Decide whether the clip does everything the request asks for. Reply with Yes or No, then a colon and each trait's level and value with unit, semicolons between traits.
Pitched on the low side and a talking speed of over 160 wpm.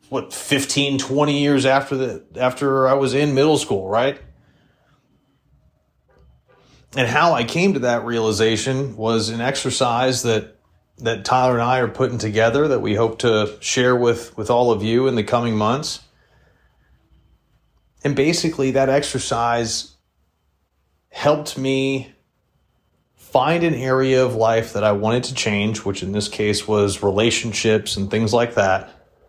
No: low, 120 Hz; average, 145 wpm